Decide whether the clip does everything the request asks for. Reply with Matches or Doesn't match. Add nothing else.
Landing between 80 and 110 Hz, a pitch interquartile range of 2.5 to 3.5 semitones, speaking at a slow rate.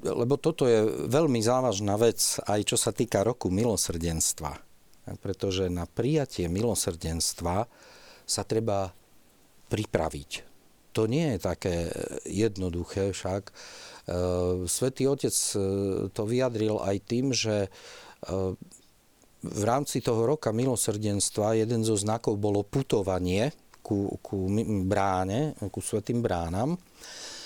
Doesn't match